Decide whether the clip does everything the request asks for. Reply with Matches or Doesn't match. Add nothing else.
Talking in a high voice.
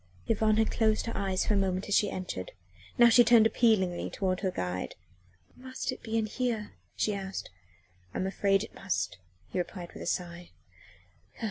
Matches